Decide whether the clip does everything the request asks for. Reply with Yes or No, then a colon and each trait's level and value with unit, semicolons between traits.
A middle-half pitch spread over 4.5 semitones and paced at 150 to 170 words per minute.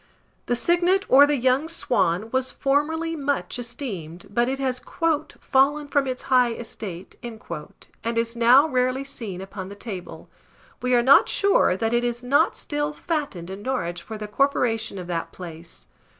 Yes: average, 5.3 semitones; average, 165 wpm